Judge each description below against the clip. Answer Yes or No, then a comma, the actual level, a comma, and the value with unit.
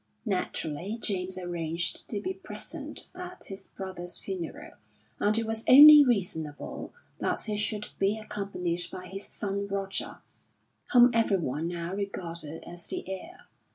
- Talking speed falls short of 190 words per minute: Yes, slow, 135 wpm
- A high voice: Yes, high, 195 Hz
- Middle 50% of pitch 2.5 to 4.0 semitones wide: Yes, average, 3.6 semitones